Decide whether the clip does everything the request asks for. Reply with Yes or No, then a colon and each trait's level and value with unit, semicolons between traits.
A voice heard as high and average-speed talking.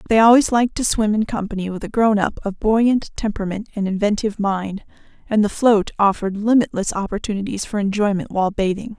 Yes: high, 210 Hz; average, 180 wpm